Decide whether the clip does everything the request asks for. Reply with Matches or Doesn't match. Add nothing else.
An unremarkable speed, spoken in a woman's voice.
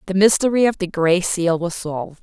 Doesn't match